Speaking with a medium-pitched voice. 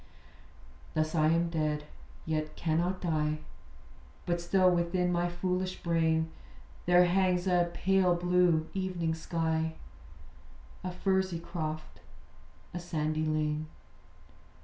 Yes: medium, 170 Hz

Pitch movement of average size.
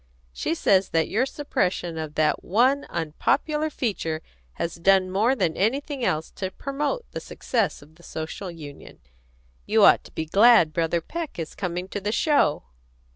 No: wide, 7.5 semitones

